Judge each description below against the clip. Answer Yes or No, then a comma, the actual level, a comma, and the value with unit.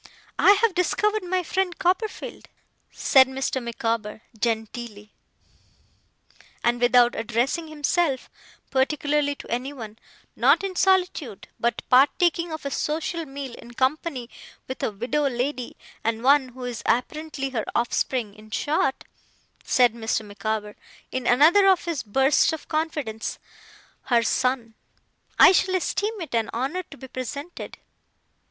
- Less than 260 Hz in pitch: No, very high, 265 Hz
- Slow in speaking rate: Yes, slow, 130 wpm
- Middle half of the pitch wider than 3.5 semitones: Yes, average, 5.1 semitones